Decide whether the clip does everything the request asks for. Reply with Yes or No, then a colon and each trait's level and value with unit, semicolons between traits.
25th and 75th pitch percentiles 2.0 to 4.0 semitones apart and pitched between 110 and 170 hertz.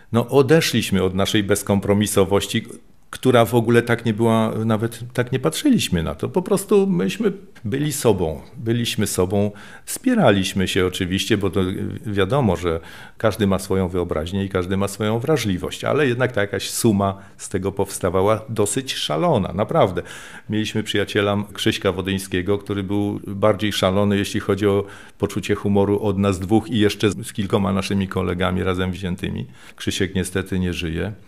No: average, 2.9 semitones; low, 100 Hz